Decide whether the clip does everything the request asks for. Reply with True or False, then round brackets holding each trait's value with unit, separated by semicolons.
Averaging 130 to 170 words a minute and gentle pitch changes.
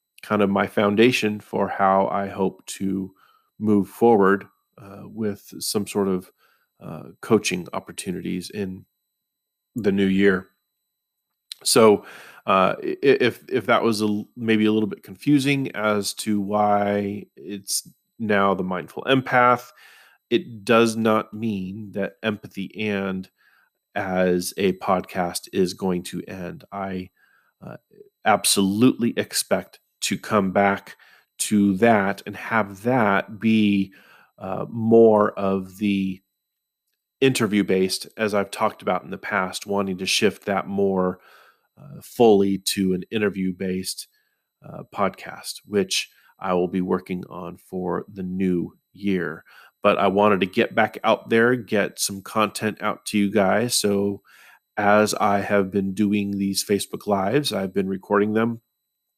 True (135 wpm; 2.0 semitones)